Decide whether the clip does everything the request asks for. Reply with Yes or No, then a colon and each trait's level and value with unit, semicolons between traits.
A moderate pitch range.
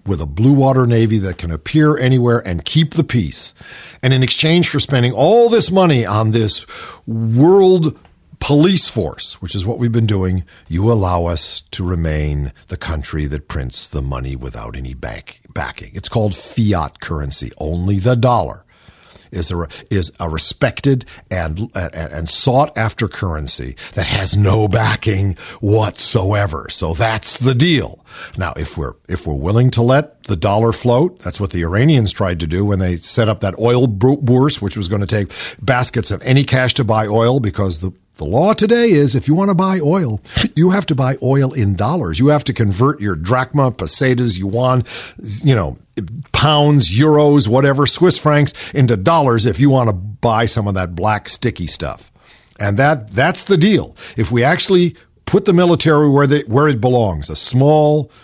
No: wide, 6.7 semitones